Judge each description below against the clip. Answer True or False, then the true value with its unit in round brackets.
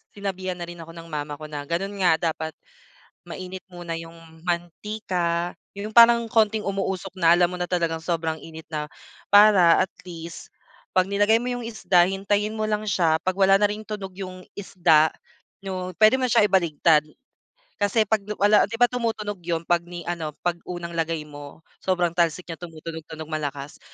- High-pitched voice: False (180 Hz)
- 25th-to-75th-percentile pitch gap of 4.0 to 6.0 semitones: False (3.6 semitones)